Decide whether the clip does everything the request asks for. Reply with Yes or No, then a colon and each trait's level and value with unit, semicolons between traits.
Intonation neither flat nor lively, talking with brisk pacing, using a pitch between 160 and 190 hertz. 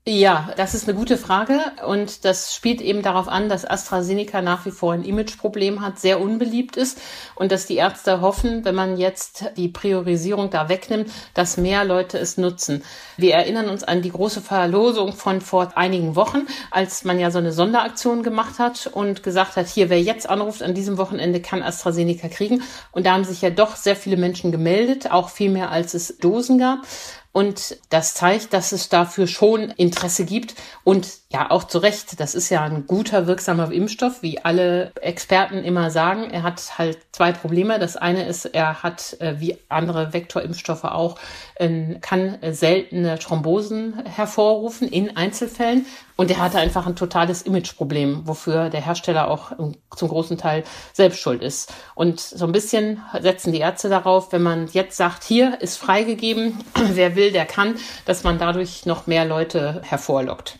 No: average, 3.0 semitones; average, 175 wpm; medium, 185 Hz